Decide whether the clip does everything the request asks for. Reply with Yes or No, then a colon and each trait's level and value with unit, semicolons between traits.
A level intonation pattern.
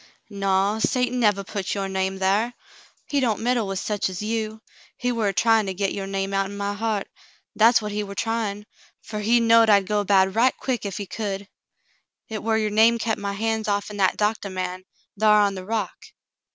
Yes: narrow, 2.3 semitones